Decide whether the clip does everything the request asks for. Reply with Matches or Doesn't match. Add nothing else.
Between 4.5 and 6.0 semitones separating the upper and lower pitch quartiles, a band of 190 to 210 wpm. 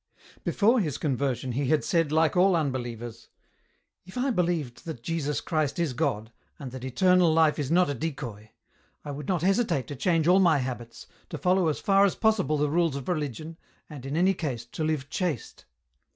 Matches